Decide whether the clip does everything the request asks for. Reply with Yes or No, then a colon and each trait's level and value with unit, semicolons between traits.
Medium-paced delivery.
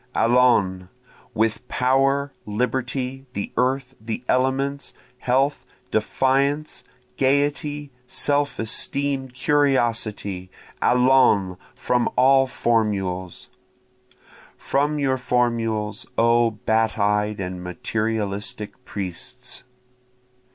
No: slow, 80 wpm